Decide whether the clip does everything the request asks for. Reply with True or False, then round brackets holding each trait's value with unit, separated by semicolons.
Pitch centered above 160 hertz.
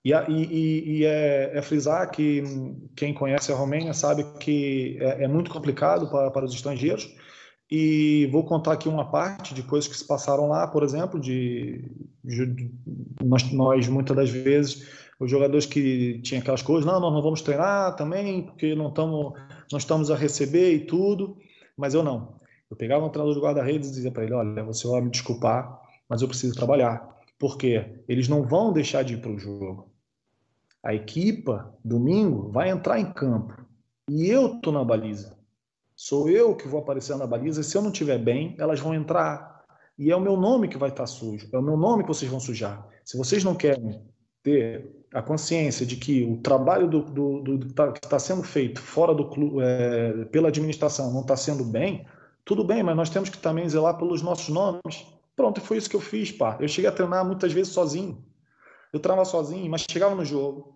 False (145 Hz)